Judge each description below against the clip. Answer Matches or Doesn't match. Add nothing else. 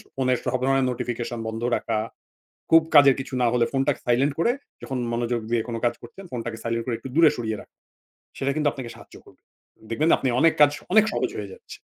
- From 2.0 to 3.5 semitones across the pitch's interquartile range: Matches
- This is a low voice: Matches